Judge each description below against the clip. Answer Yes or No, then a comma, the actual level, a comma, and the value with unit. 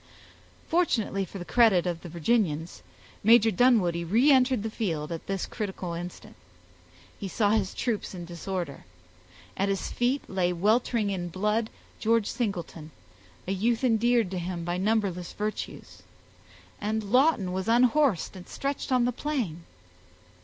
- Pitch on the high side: Yes, high, 205 Hz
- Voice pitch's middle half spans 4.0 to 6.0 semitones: Yes, average, 4.8 semitones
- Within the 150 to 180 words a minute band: No, average, 140 wpm